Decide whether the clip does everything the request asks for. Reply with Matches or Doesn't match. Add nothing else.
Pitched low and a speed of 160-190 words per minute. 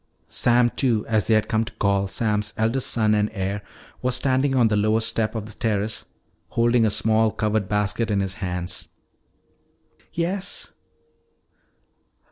Doesn't match